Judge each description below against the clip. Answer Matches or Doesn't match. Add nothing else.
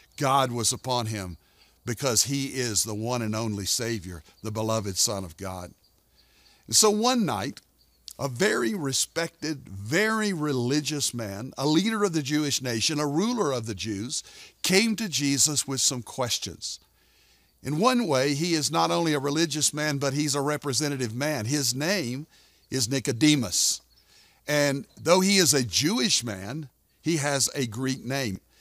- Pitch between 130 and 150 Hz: Matches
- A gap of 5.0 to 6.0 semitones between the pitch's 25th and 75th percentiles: Matches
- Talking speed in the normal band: Matches